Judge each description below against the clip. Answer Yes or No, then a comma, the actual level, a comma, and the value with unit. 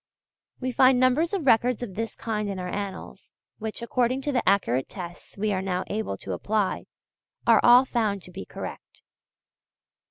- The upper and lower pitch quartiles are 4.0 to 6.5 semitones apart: Yes, average, 4.5 semitones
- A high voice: Yes, high, 220 Hz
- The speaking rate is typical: Yes, average, 170 wpm